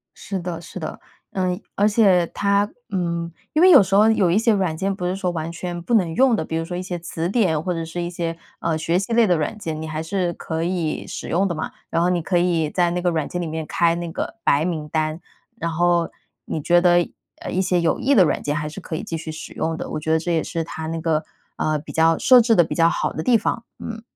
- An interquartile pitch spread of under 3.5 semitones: Yes, narrow, 2.5 semitones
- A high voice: No, medium, 175 Hz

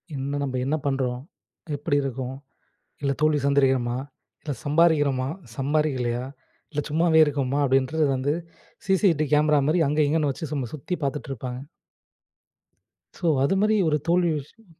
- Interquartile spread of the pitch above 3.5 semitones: No, average, 2.8 semitones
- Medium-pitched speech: Yes, medium, 145 Hz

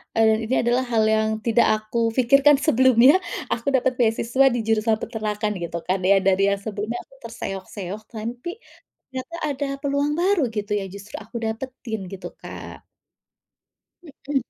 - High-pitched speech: Yes, high, 225 Hz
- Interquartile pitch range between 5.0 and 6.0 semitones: No, average, 3.5 semitones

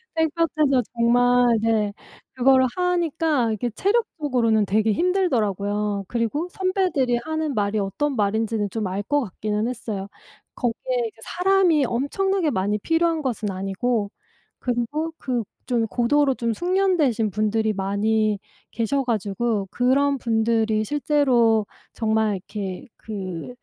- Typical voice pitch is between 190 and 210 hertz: No, high, 235 Hz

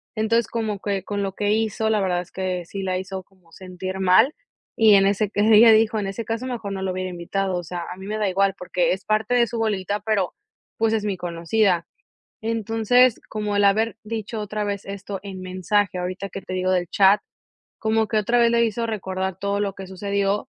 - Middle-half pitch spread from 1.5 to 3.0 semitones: Yes, average, 2.7 semitones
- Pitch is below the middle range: No, high, 200 Hz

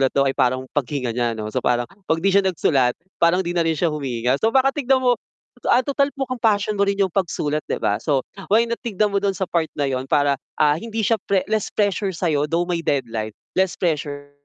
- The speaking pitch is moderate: Yes, medium, 170 Hz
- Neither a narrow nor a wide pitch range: No, wide, 6.4 semitones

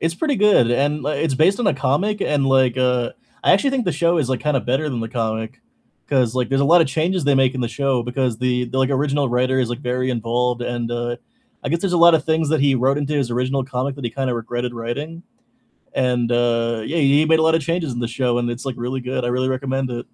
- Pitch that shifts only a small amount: No, average, 3.5 semitones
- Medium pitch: No, low, 130 Hz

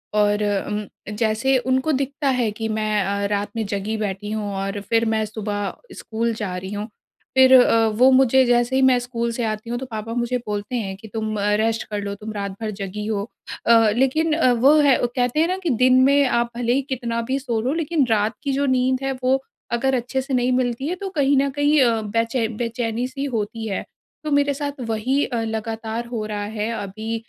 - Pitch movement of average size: Yes, average, 3.5 semitones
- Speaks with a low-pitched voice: No, high, 230 Hz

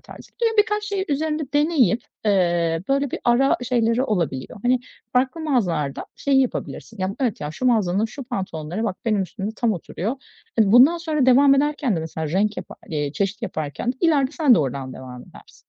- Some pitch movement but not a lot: No, wide, 7.7 semitones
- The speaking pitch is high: Yes, high, 230 Hz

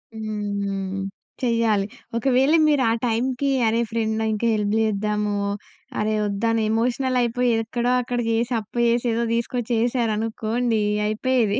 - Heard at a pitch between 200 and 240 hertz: Yes, high, 225 Hz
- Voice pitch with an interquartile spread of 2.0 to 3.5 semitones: Yes, narrow, 2.4 semitones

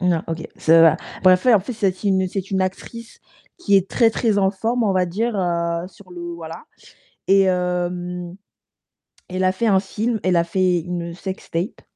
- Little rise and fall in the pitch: Yes, narrow, 2.3 semitones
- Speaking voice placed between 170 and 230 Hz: Yes, medium, 185 Hz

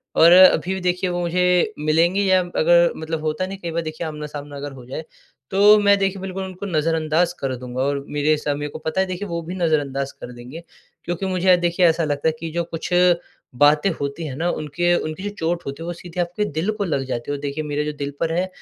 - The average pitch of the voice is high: No, medium, 165 Hz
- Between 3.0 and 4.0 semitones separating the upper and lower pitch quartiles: Yes, average, 3.4 semitones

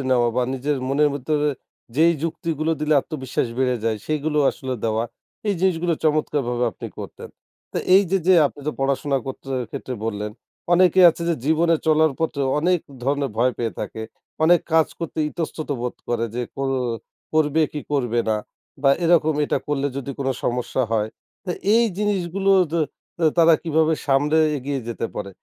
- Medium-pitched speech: Yes, medium, 150 Hz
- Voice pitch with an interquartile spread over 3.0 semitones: Yes, average, 3.9 semitones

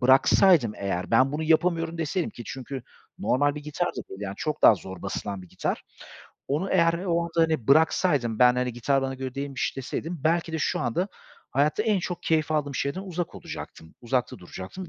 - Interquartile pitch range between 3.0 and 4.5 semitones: No, average, 5.1 semitones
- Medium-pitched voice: Yes, medium, 145 Hz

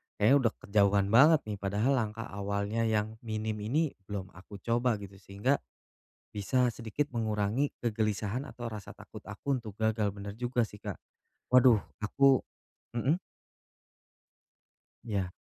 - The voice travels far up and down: No, average, 3.1 semitones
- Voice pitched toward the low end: Yes, low, 110 Hz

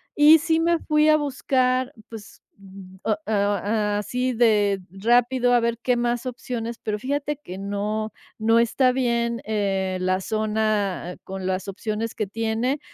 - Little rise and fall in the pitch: No, average, 3.6 semitones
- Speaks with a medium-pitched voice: No, high, 225 Hz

